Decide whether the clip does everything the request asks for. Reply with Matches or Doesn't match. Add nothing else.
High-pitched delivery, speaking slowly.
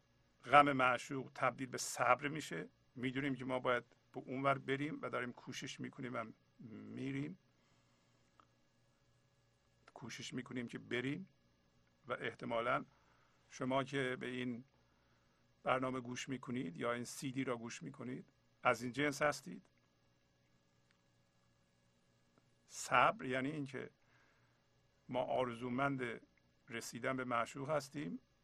Doesn't match